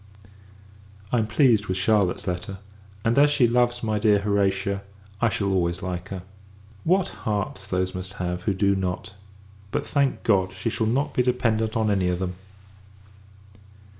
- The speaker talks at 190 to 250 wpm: No, average, 165 wpm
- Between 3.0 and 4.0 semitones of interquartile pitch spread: Yes, average, 3.5 semitones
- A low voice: Yes, low, 100 Hz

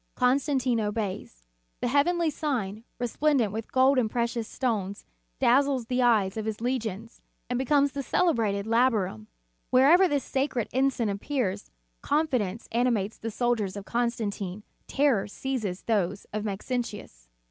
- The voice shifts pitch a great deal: No, average, 4.2 semitones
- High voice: Yes, high, 235 Hz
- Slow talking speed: Yes, slow, 130 wpm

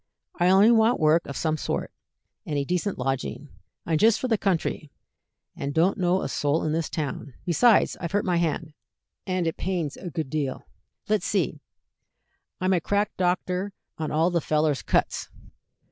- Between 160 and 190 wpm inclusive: Yes, average, 175 wpm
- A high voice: No, medium, 170 Hz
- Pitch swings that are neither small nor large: Yes, average, 3.6 semitones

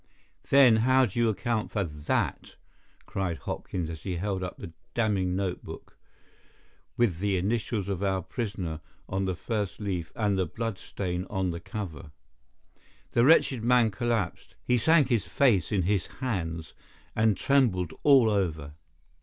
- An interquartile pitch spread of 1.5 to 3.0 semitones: No, average, 4.5 semitones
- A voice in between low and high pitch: No, low, 100 Hz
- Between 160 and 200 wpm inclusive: No, average, 150 wpm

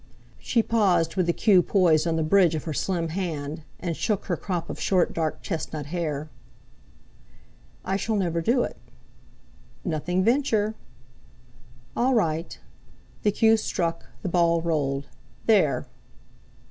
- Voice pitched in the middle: Yes, medium, 175 Hz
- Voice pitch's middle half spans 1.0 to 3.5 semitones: No, average, 3.9 semitones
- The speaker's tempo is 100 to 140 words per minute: Yes, slow, 135 wpm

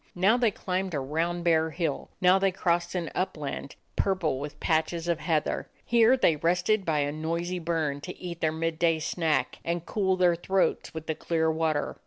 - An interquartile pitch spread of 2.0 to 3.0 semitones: Yes, narrow, 2.4 semitones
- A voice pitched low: No, medium, 170 Hz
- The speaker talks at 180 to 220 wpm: Yes, average, 185 wpm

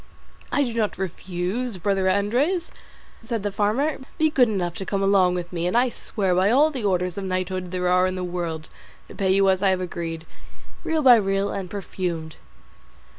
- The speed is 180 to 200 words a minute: Yes, average, 195 wpm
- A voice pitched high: Yes, high, 195 Hz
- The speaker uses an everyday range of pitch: Yes, average, 3.5 semitones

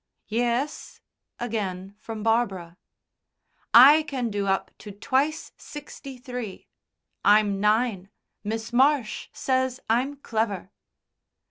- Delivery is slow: Yes, slow, 100 wpm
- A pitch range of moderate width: Yes, average, 4.1 semitones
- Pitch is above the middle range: Yes, high, 230 Hz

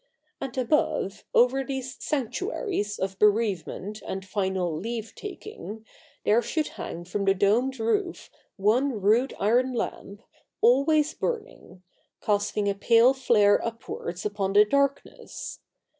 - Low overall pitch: No, high, 225 Hz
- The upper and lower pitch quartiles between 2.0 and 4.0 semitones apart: No, average, 4.9 semitones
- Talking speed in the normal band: No, slow, 125 wpm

